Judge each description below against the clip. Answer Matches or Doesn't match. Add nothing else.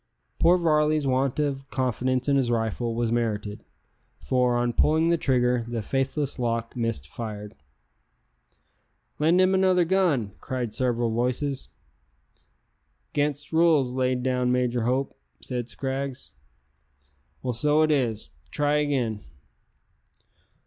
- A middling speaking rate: Doesn't match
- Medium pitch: Doesn't match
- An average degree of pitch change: Matches